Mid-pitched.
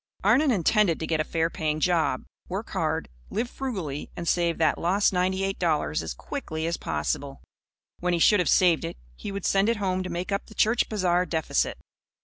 Yes: medium, 180 Hz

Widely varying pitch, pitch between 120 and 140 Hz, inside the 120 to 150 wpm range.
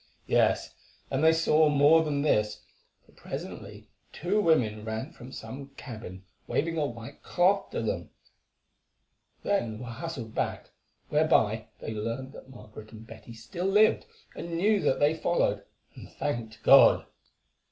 Yes: wide, 6.5 semitones; low, 135 Hz; average, 140 wpm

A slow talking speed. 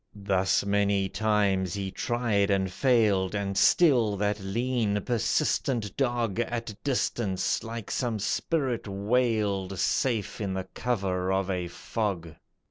Yes: slow, 125 wpm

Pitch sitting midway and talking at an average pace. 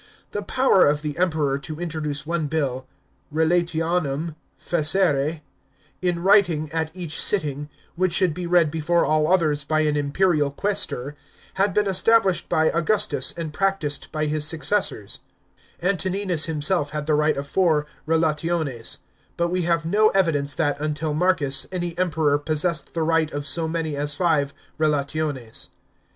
Yes: medium, 160 Hz; average, 150 wpm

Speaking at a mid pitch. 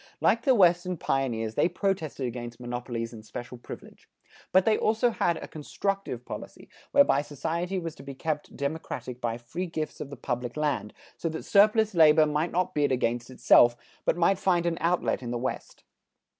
Yes: medium, 155 Hz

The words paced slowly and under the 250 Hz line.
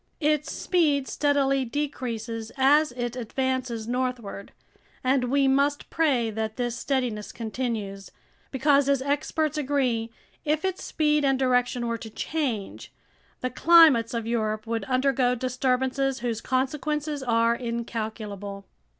No: slow, 125 wpm; very high, 255 Hz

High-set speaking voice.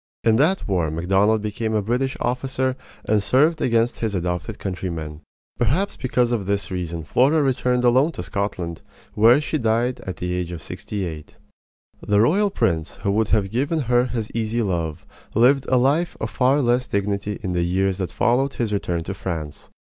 No: low, 110 Hz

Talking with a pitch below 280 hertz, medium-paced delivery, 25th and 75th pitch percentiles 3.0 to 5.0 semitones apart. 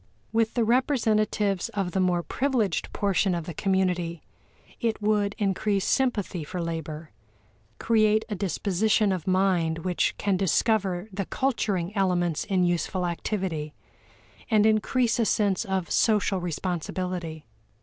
No: high, 190 Hz; slow, 130 wpm; average, 3.4 semitones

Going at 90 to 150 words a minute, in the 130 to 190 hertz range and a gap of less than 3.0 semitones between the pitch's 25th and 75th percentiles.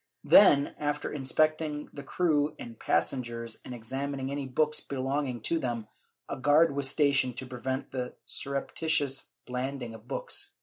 Yes: average, 140 wpm; low, 135 Hz; narrow, 2.6 semitones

